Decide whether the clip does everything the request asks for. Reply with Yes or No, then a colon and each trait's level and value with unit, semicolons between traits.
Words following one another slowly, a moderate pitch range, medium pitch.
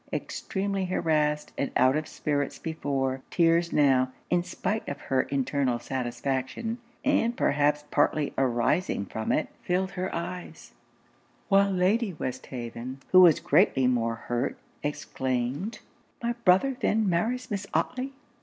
No: slow, 125 wpm; wide, 6.3 semitones; medium, 150 Hz